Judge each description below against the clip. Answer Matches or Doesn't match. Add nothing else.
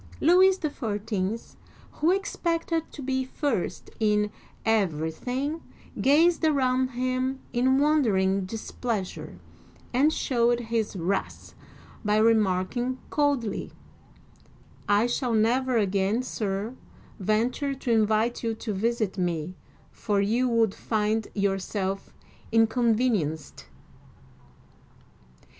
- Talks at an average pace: Doesn't match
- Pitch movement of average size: Matches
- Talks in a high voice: Matches